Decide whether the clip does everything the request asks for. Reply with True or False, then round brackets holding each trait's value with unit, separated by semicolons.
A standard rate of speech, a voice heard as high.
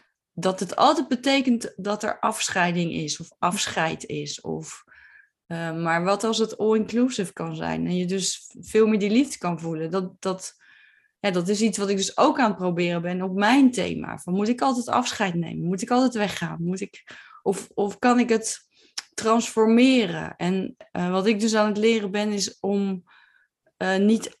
True (190 wpm; 200 Hz)